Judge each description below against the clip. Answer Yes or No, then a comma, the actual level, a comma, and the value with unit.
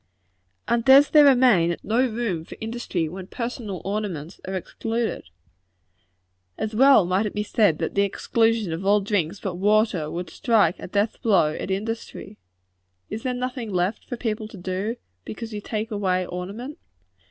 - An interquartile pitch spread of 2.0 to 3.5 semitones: No, average, 3.9 semitones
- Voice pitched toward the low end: No, high, 210 Hz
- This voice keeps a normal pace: Yes, average, 165 wpm